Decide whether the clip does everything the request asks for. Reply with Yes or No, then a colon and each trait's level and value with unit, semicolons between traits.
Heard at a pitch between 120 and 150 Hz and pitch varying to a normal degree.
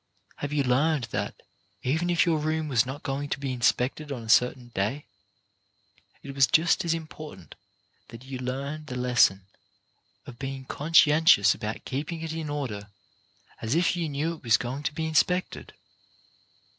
Yes: medium, 140 Hz; average, 3.9 semitones